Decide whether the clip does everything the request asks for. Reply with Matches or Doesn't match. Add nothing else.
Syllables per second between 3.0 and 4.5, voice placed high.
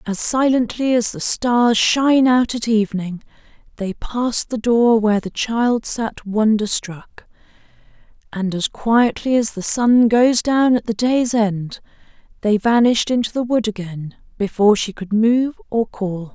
Matches